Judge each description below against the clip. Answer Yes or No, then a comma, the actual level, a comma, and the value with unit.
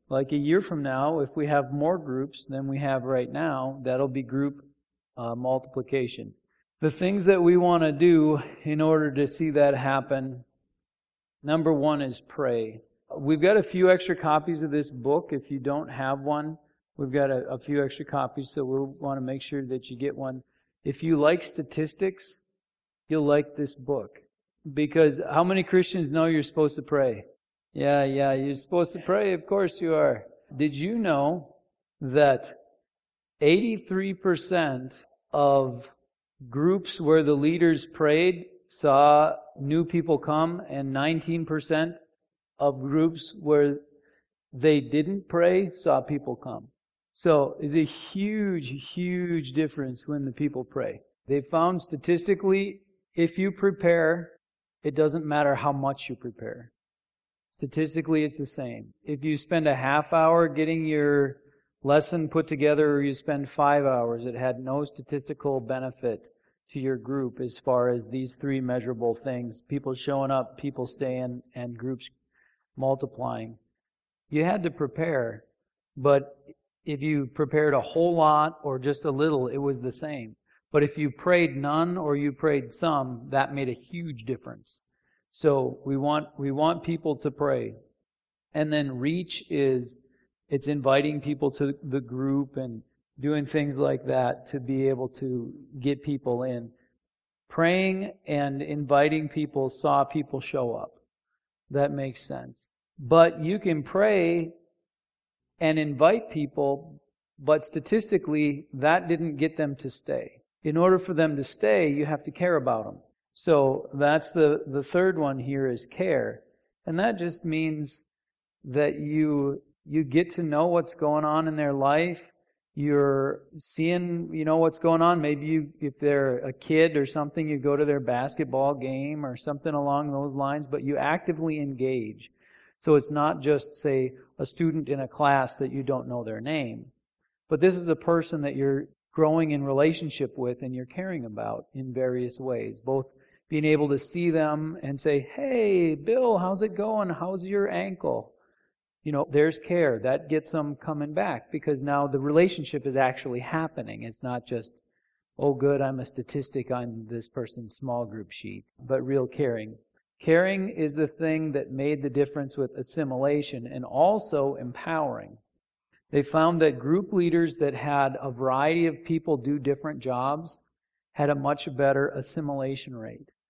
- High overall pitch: No, medium, 145 Hz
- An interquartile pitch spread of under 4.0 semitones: Yes, average, 2.9 semitones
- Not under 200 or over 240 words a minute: No, average, 160 wpm